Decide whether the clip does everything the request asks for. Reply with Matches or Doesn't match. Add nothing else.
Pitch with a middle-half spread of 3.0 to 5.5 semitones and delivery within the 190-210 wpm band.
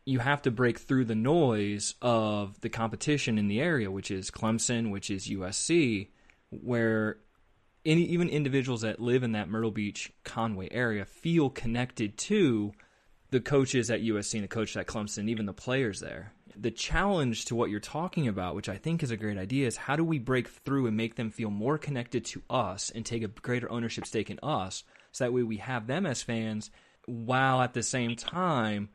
Matches